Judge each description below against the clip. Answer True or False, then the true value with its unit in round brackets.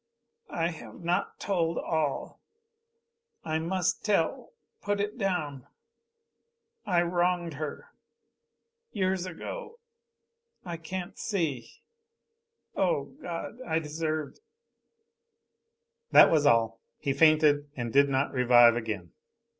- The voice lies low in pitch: False (165 Hz)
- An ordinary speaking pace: False (105 wpm)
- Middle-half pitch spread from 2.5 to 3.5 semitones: False (4.8 semitones)